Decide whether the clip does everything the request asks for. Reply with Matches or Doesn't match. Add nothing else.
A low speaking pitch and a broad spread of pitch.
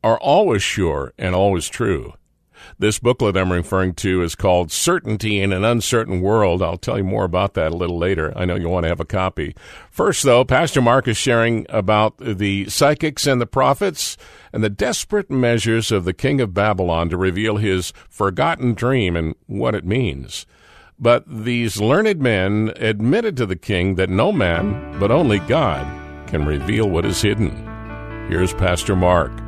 Doesn't match